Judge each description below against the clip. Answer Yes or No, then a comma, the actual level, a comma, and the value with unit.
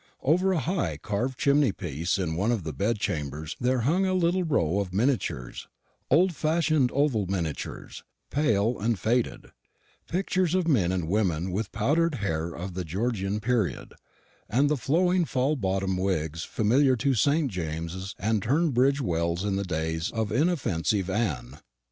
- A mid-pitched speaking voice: No, low, 110 Hz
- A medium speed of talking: Yes, average, 155 wpm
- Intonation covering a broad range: Yes, wide, 7.8 semitones